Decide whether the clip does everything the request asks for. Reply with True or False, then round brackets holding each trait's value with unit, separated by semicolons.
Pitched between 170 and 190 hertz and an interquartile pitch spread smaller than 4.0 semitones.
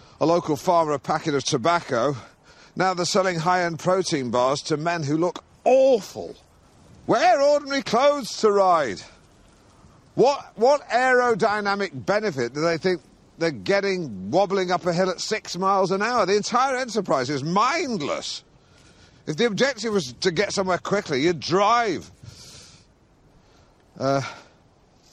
False (185 Hz; 4.6 semitones)